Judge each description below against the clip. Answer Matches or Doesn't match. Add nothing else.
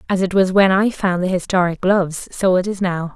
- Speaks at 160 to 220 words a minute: Doesn't match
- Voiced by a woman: Matches